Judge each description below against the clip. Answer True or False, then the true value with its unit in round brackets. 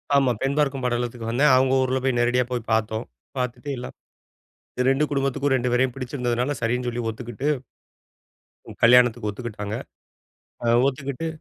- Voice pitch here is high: False (125 Hz)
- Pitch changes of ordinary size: False (2.1 semitones)